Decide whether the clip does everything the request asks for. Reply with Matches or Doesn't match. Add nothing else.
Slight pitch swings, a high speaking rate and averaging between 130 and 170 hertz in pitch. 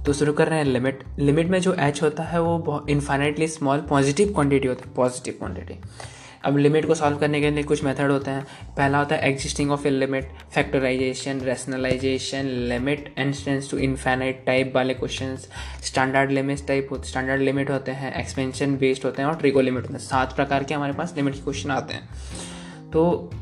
Matches